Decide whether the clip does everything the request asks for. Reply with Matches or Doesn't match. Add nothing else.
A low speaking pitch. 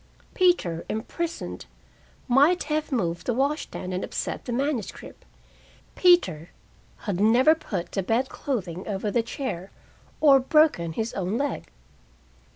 Doesn't match